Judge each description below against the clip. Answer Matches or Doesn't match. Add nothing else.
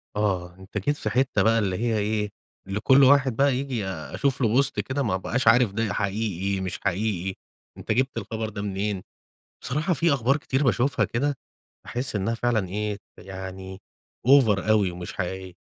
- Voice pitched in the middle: Doesn't match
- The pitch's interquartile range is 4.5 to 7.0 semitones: Matches